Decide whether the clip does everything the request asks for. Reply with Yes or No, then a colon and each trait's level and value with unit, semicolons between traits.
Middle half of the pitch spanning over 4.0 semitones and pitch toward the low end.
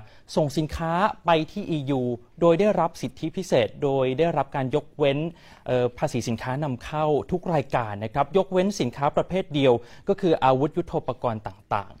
No: average, 4.7 semitones; medium, 150 Hz